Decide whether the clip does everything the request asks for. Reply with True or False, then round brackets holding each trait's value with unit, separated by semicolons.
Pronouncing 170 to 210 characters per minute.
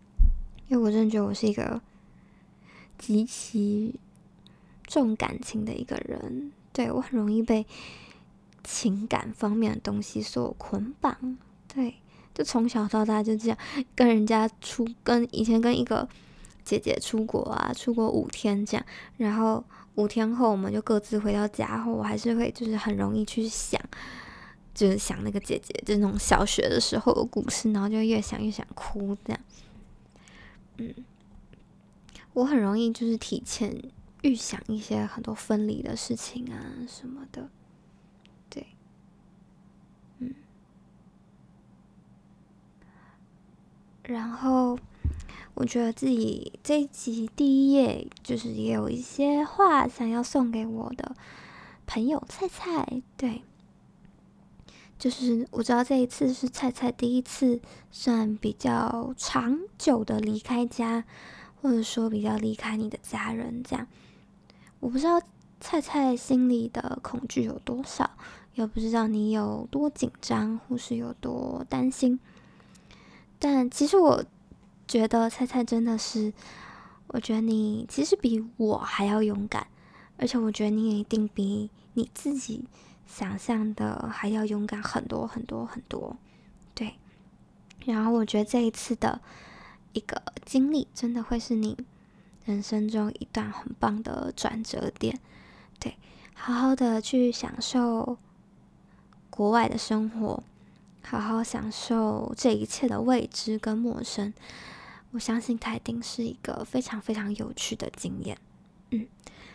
True (200 characters per minute)